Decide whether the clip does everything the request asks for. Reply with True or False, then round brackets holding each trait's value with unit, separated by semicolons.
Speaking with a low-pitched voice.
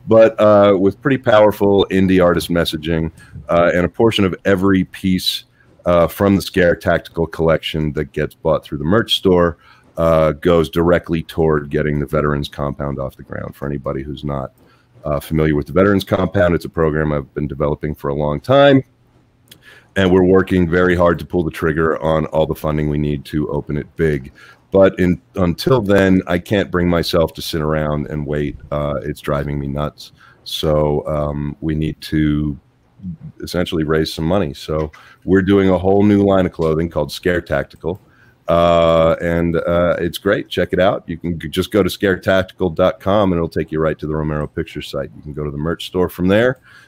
True (85 Hz)